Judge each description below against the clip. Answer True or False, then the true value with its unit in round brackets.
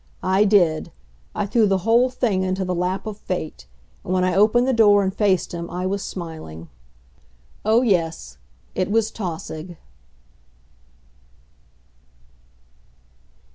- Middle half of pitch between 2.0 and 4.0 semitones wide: True (3.4 semitones)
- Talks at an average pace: False (130 wpm)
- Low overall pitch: False (190 Hz)